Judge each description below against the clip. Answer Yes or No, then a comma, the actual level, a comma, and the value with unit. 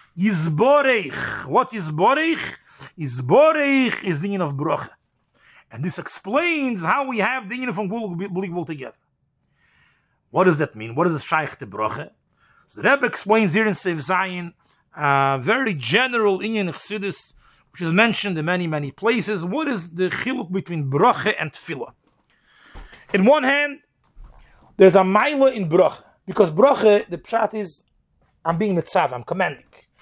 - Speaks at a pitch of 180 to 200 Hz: Yes, high, 190 Hz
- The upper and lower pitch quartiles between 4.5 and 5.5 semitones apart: Yes, average, 5.0 semitones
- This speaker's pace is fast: No, average, 155 wpm